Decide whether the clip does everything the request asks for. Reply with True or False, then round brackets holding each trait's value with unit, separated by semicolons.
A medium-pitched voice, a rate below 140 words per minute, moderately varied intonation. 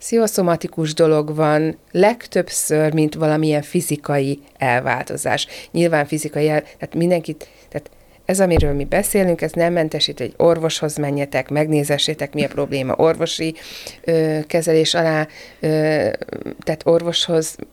False (155 Hz; 120 wpm; 1.9 semitones)